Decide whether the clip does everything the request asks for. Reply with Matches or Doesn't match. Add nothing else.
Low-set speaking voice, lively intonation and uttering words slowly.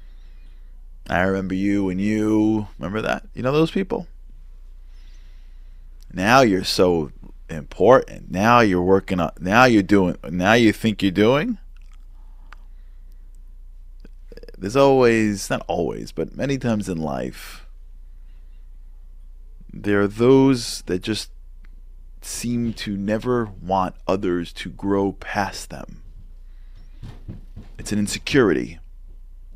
Matches